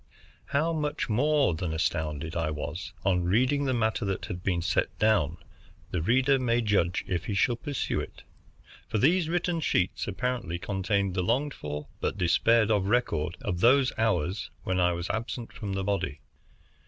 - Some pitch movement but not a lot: No, wide, 6.1 semitones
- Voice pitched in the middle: No, low, 100 Hz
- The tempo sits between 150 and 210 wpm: Yes, average, 170 wpm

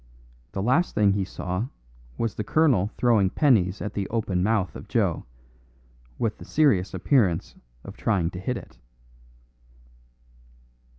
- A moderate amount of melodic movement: Yes, average, 4.2 semitones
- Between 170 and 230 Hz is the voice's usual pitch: No, low, 105 Hz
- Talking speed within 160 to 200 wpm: No, slow, 135 wpm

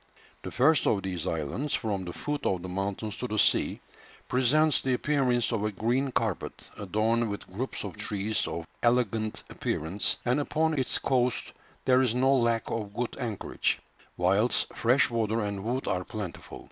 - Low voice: Yes, low, 115 Hz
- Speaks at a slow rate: No, average, 170 wpm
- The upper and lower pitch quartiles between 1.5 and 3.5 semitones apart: No, average, 4.0 semitones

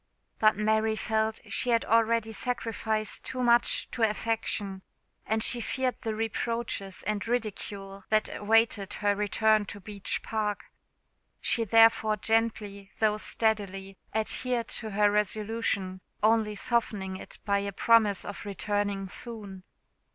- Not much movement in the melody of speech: Yes, narrow, 1.8 semitones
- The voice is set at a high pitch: Yes, high, 215 Hz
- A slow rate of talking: Yes, slow, 130 wpm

